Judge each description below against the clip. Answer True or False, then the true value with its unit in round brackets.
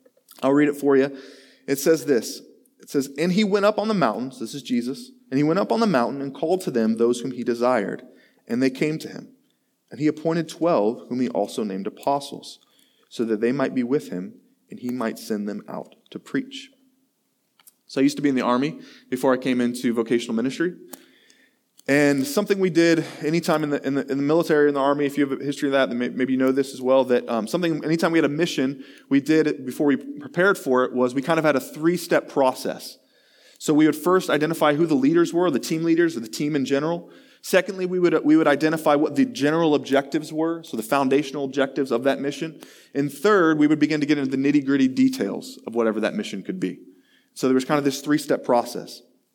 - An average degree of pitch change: True (3.9 semitones)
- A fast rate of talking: True (235 wpm)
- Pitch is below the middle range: False (145 Hz)